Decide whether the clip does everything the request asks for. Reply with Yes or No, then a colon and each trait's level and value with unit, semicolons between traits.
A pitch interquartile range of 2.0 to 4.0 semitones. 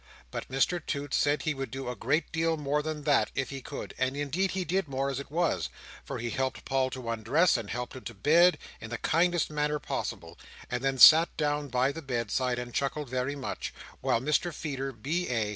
Yes: average, 3.3 semitones